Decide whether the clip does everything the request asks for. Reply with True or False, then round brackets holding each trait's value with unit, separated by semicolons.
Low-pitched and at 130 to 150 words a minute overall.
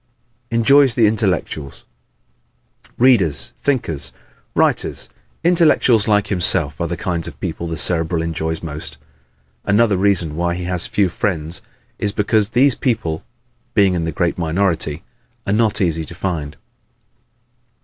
True (90 Hz; 135 wpm)